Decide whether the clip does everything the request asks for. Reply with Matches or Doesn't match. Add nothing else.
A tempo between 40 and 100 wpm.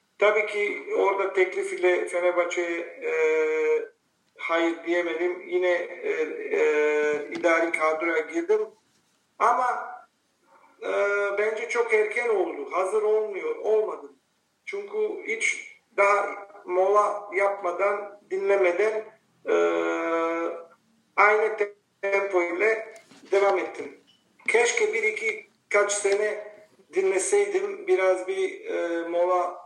Matches